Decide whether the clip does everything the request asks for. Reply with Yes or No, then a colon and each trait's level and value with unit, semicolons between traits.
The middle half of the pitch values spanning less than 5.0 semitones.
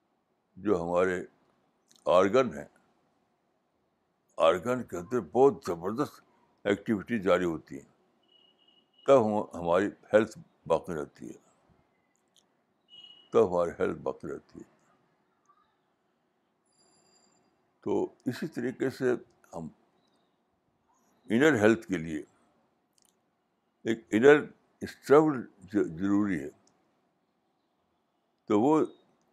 No: wide, 5.5 semitones